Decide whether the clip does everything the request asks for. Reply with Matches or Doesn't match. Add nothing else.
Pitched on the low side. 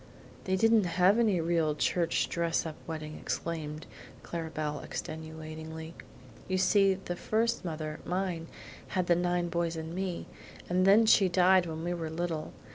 Doesn't match